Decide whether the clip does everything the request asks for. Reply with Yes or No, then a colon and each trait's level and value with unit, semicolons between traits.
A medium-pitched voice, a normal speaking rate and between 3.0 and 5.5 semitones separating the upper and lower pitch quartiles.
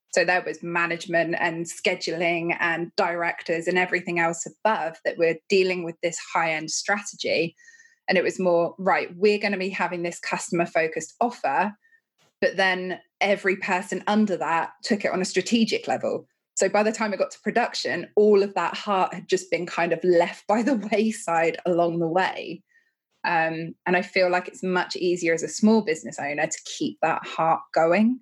Yes: medium, 180 Hz; average, 185 wpm; average, 3.4 semitones